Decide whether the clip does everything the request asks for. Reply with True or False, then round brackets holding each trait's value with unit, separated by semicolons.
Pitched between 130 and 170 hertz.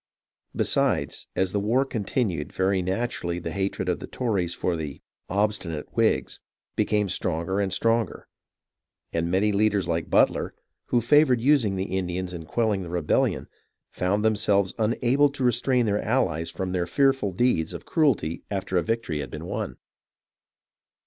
False (100 Hz)